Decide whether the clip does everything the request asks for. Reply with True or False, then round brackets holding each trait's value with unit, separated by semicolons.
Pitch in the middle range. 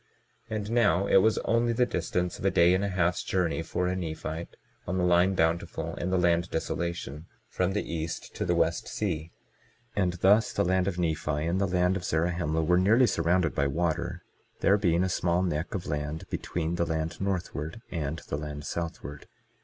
False (85 Hz)